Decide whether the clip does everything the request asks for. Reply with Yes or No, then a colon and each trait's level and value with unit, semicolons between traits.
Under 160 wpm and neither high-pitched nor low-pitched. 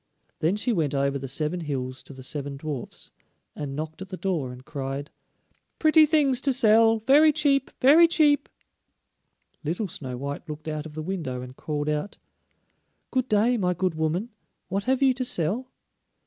No: average, 175 wpm; medium, 170 Hz